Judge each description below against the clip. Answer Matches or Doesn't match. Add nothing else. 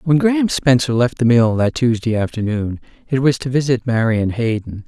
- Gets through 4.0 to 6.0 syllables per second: Matches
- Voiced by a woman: Doesn't match